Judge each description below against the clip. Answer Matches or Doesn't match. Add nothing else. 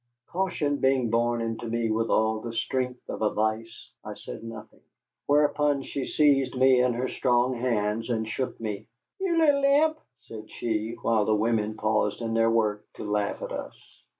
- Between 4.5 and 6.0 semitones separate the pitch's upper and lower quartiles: Doesn't match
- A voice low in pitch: Matches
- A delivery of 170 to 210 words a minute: Matches